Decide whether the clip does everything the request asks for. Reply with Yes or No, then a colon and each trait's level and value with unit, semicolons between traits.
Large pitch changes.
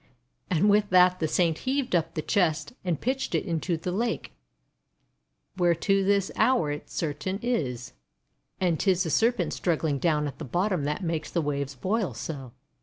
No: average, 4.6 semitones